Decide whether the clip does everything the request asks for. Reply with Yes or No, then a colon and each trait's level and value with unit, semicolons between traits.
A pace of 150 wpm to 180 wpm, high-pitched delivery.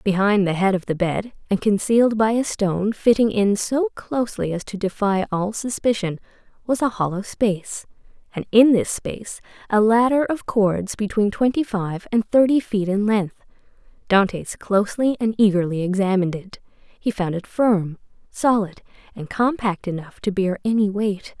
Yes: average, 165 wpm; high, 210 Hz